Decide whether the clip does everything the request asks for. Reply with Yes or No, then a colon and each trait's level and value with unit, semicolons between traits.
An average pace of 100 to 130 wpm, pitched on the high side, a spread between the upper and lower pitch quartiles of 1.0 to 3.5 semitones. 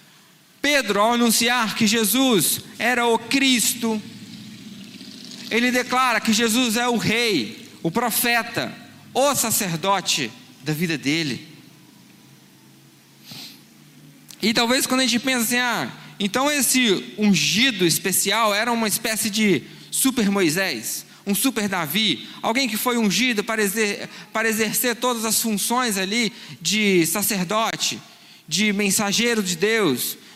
Yes: slow, 120 wpm; high, 220 Hz; average, 3.2 semitones